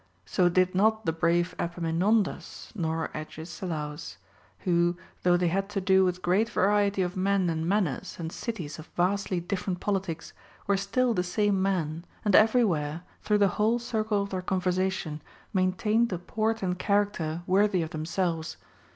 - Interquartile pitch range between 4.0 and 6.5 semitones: No, average, 3.1 semitones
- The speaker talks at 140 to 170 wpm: Yes, average, 160 wpm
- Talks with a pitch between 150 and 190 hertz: Yes, medium, 185 Hz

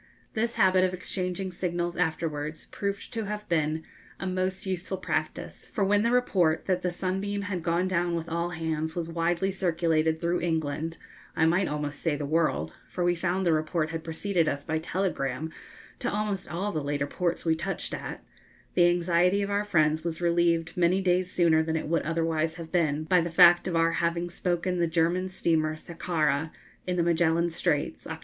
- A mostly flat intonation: Yes, narrow, 2.3 semitones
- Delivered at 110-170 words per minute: No, average, 190 wpm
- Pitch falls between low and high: Yes, medium, 170 Hz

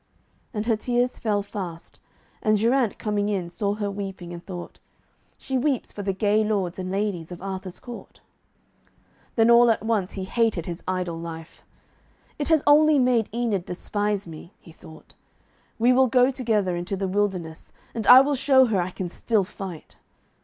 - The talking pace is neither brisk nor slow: Yes, average, 175 wpm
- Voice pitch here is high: Yes, high, 205 Hz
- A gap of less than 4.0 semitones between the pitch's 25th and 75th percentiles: No, average, 4.4 semitones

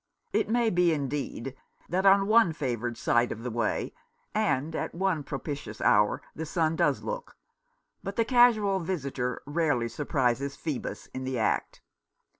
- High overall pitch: No, medium, 150 Hz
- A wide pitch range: Yes, wide, 7.2 semitones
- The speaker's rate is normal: Yes, average, 150 wpm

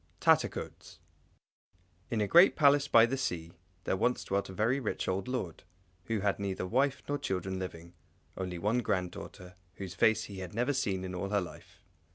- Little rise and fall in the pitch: No, average, 4.9 semitones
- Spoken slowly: No, average, 185 wpm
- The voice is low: Yes, low, 100 Hz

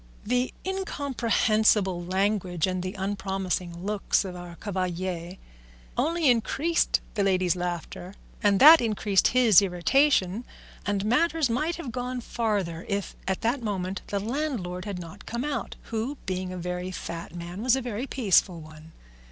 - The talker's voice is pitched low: No, high, 200 Hz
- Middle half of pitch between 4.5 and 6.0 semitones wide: Yes, average, 5.2 semitones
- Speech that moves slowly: No, average, 145 wpm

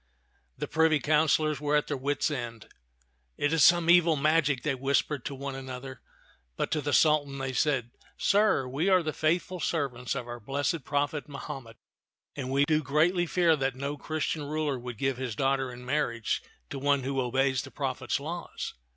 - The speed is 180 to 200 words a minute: Yes, average, 185 wpm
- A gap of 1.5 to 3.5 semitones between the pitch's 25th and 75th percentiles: Yes, average, 2.8 semitones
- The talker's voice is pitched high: No, medium, 140 Hz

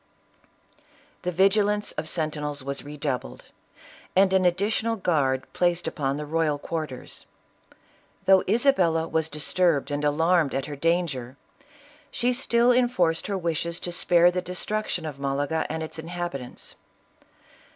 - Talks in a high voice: No, medium, 165 Hz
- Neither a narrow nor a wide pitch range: Yes, average, 3.9 semitones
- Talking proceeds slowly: Yes, slow, 130 wpm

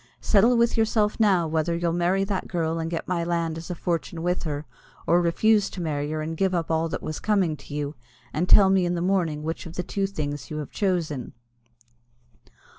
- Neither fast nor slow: No, fast, 215 wpm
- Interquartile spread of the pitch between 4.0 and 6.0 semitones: No, average, 3.2 semitones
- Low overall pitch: No, medium, 170 Hz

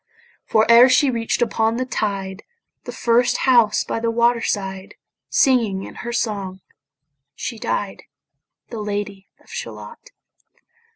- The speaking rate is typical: No, slow, 130 wpm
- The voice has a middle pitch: No, high, 225 Hz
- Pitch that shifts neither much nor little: Yes, average, 3.0 semitones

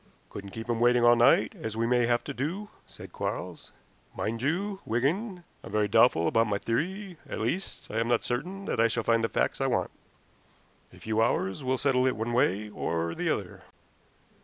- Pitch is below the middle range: Yes, low, 120 Hz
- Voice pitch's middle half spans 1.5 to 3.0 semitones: No, average, 3.9 semitones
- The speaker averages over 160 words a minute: Yes, average, 200 wpm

